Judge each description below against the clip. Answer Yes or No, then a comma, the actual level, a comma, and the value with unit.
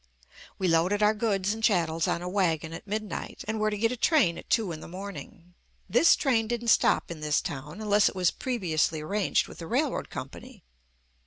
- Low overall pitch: No, high, 200 Hz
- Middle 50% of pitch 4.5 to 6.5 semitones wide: Yes, average, 4.8 semitones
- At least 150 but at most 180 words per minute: No, average, 200 wpm